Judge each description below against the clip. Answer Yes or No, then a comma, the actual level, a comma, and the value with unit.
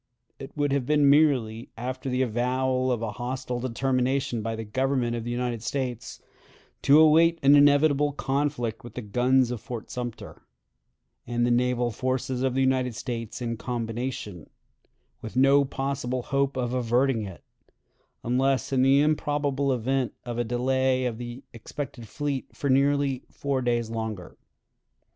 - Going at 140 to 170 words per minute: Yes, average, 155 wpm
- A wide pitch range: No, narrow, 2.4 semitones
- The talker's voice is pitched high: No, low, 130 Hz